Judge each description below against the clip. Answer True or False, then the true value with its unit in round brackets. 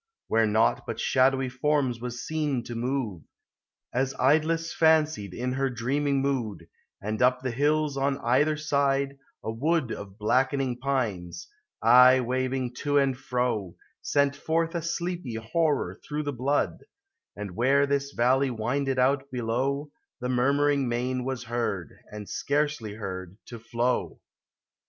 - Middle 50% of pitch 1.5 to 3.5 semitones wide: True (3.2 semitones)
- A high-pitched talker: False (130 Hz)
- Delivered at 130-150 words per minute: True (140 wpm)